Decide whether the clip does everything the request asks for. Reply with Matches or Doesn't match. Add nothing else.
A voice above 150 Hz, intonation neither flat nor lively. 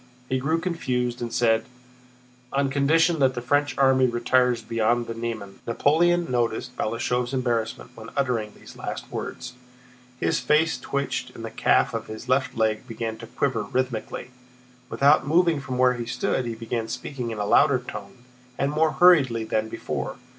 Doesn't match